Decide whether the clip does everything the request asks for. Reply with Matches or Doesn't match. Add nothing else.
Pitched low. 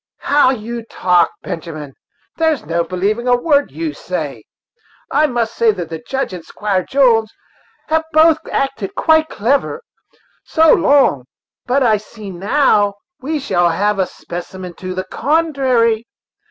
Doesn't match